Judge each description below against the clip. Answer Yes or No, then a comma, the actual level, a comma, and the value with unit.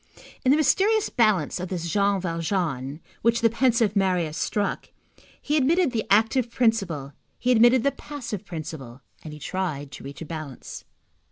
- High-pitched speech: Yes, high, 200 Hz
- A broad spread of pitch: Yes, wide, 7.1 semitones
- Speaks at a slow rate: No, average, 160 wpm